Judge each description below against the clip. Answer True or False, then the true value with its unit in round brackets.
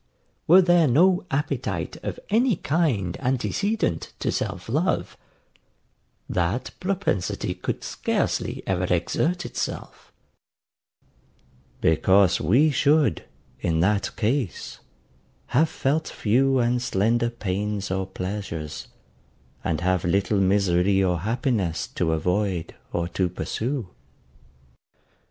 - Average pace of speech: False (100 wpm)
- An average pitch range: False (7.3 semitones)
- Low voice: True (105 Hz)